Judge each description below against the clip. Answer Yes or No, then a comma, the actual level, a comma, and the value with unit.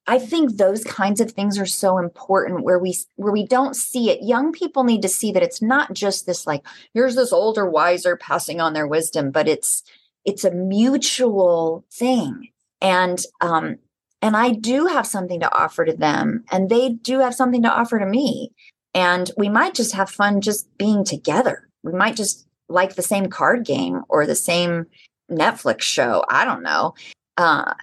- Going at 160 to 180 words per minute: No, average, 190 wpm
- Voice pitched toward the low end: No, high, 205 Hz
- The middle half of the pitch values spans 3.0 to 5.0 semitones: No, wide, 5.5 semitones